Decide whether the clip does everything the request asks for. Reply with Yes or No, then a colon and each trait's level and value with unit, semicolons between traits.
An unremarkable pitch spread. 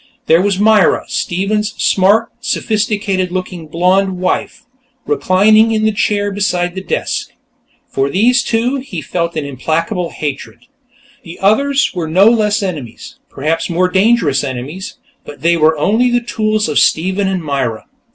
Yes: average, 4.5 semitones